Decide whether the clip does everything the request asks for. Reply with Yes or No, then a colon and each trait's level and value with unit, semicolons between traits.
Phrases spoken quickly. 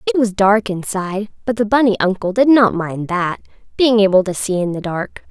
Yes: fast, 215 wpm